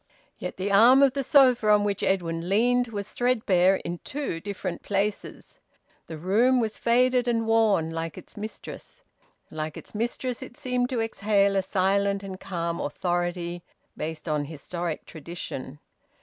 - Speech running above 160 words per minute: No, average, 150 wpm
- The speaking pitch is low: No, high, 200 Hz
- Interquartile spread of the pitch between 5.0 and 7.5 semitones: Yes, average, 5.3 semitones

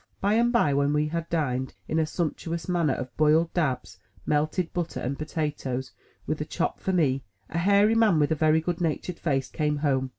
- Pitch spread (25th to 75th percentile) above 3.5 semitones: No, average, 3.1 semitones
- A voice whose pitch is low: No, medium, 155 Hz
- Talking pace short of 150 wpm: No, average, 200 wpm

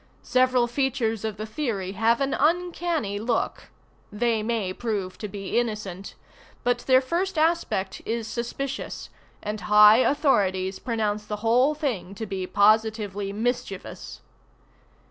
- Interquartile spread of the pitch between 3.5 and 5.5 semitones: Yes, average, 3.9 semitones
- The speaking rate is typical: No, slow, 125 wpm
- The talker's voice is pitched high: Yes, high, 225 Hz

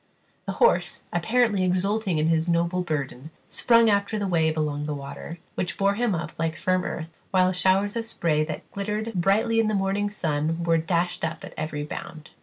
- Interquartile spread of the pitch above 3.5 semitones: Yes, average, 4.2 semitones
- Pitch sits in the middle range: Yes, medium, 180 Hz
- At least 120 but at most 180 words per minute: No, average, 190 wpm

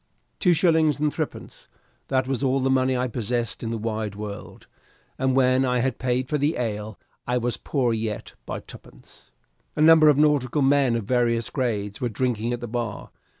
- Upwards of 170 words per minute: Yes, average, 190 wpm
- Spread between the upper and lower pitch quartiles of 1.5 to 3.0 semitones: Yes, average, 2.7 semitones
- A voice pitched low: Yes, low, 125 Hz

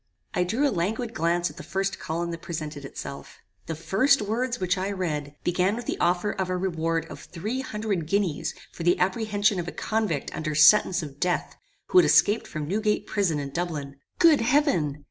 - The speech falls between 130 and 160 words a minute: No, average, 195 wpm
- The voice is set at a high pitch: No, medium, 180 Hz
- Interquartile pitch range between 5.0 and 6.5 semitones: No, average, 4.6 semitones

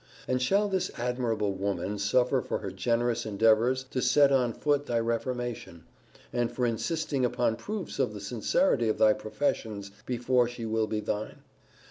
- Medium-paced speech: Yes, average, 160 wpm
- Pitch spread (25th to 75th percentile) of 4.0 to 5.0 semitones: No, average, 3.0 semitones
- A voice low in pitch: Yes, low, 120 Hz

